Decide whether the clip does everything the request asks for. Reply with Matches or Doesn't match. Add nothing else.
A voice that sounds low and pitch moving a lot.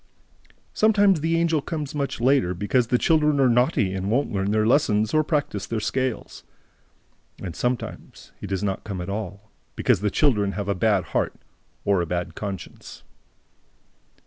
Matches